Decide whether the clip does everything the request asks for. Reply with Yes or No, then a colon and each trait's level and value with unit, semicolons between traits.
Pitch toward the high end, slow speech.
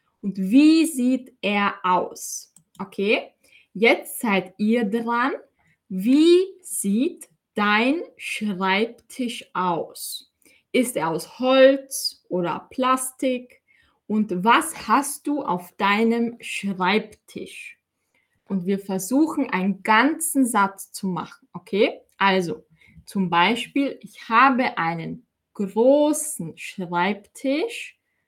Yes: high, 225 Hz; slow, 95 wpm